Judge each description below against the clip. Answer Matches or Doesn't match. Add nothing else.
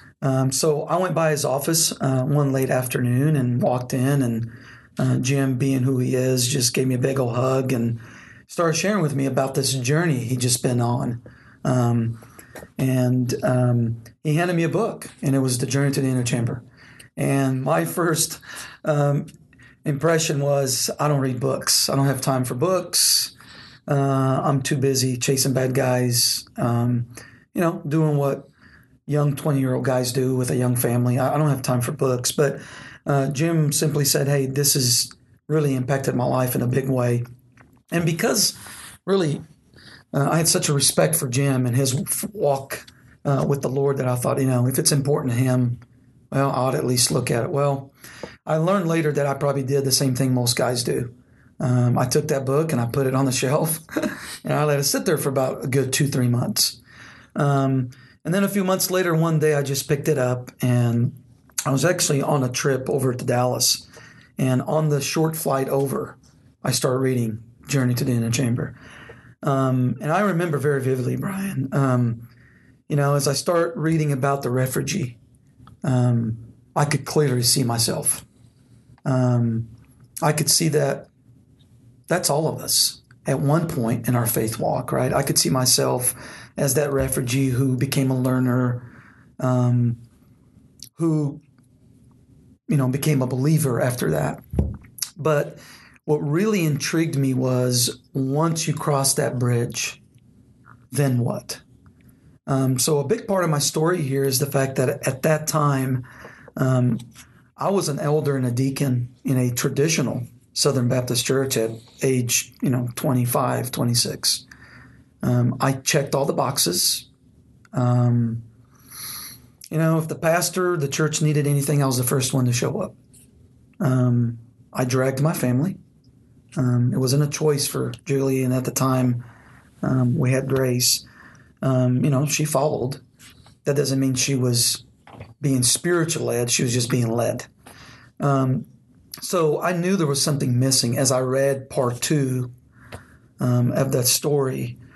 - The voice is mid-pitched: Doesn't match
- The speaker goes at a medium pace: Matches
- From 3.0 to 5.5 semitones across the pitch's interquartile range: Doesn't match